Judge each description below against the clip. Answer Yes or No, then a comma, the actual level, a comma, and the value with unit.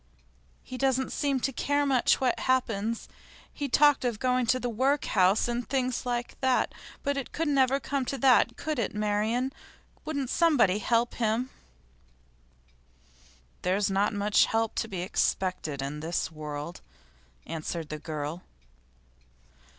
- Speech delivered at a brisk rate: No, average, 140 wpm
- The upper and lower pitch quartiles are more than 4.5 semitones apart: Yes, average, 5.1 semitones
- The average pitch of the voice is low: No, high, 240 Hz